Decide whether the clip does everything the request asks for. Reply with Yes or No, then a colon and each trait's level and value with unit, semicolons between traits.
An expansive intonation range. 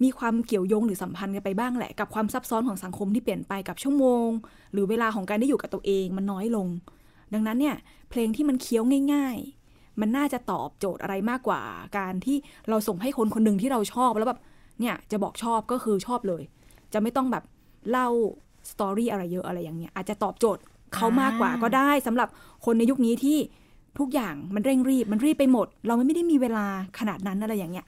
No: average, 4.0 semitones